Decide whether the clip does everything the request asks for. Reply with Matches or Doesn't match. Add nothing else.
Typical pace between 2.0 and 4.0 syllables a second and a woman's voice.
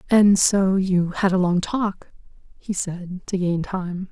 Matches